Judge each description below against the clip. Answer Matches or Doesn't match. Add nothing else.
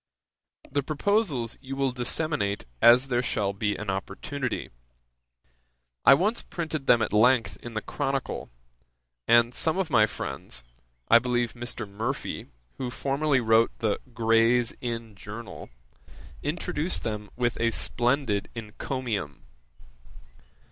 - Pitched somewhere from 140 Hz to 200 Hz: Doesn't match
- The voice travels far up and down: Doesn't match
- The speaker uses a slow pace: Matches